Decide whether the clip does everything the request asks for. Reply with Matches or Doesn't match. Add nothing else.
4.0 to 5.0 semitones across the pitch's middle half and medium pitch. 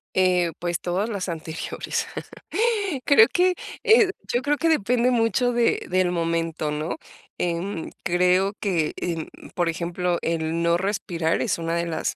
Matches